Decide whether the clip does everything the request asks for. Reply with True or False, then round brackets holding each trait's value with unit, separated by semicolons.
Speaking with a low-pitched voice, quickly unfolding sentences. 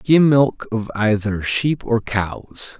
False (115 Hz; 150 wpm)